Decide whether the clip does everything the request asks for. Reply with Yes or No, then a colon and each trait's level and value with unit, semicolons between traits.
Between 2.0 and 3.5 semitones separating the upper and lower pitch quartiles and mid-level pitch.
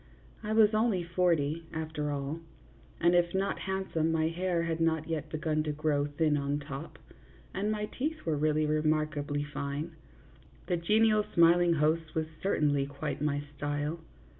Yes: average, 2.9 semitones; medium, 160 Hz